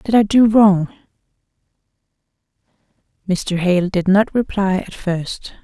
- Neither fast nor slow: No, slow, 115 wpm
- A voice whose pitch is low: No, high, 195 Hz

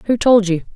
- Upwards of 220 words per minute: Yes, fast, 235 wpm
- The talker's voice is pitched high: Yes, high, 210 Hz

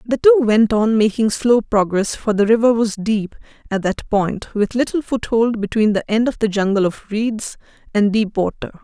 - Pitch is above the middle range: Yes, high, 220 Hz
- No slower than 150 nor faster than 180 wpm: No, average, 195 wpm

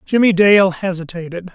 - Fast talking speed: No, slow, 115 wpm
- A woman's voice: No, male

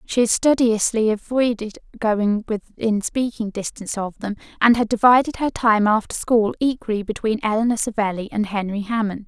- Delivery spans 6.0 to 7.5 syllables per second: No, 5.2 syllables/s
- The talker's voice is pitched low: No, high, 220 Hz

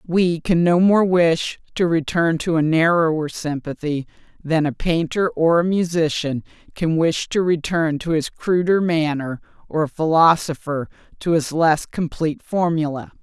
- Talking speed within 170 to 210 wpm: No, average, 150 wpm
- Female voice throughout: Yes, female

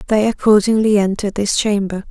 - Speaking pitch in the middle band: No, high, 205 Hz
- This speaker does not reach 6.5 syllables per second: Yes, 5.8 syllables/s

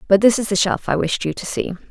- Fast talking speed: Yes, fast, 315 wpm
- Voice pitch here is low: No, high, 190 Hz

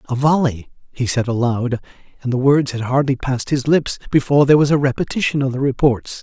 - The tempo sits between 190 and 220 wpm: Yes, fast, 205 wpm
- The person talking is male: Yes, male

